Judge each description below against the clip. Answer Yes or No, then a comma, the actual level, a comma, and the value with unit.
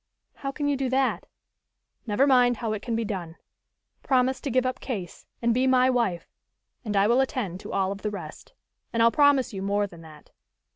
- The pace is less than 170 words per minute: No, fast, 205 wpm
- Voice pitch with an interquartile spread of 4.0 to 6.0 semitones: Yes, average, 4.6 semitones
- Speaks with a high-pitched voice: Yes, high, 235 Hz